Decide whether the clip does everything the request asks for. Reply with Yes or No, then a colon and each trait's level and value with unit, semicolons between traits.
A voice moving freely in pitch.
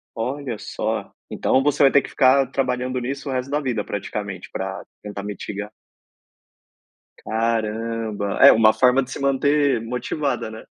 No: average, 3.7 semitones